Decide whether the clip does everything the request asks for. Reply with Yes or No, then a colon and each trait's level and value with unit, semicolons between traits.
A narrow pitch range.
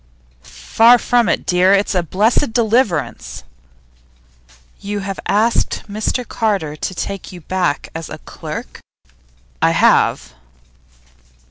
No: average, 4.0 semitones